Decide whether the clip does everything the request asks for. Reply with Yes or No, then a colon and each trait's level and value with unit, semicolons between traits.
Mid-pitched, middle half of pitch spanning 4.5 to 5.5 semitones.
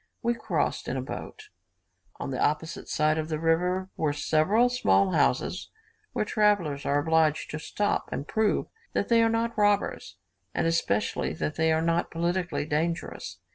Yes: medium, 165 Hz; average, 5.0 semitones